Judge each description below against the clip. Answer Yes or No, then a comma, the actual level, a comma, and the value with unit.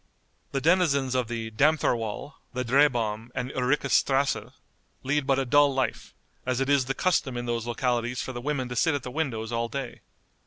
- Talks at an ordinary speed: Yes, average, 190 wpm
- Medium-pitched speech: No, low, 130 Hz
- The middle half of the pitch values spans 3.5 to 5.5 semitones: No, average, 2.8 semitones